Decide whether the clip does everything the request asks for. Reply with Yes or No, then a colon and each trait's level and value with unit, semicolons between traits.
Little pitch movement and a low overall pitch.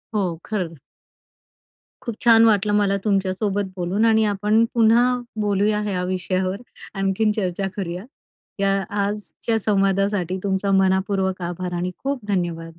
No: narrow, 2.2 semitones; high, 195 Hz